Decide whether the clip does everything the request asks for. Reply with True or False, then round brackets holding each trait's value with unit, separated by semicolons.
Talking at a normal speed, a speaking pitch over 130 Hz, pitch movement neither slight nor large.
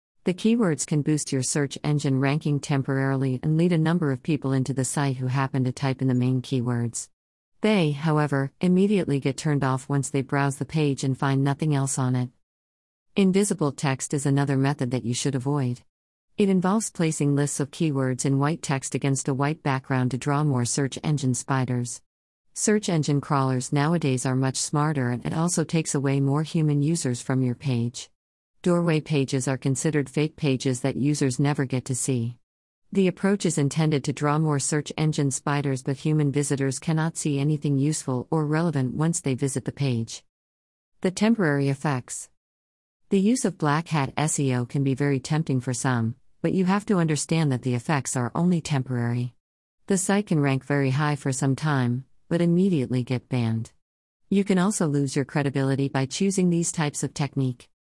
True (185 wpm; 140 Hz; 3.1 semitones)